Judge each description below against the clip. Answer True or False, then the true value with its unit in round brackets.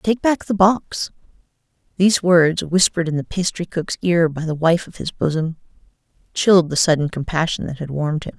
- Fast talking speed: False (185 wpm)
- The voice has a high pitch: False (170 Hz)